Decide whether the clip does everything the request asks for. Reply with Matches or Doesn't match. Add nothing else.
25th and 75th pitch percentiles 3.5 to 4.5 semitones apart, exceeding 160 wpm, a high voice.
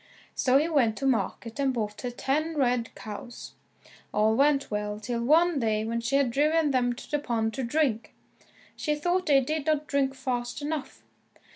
Matches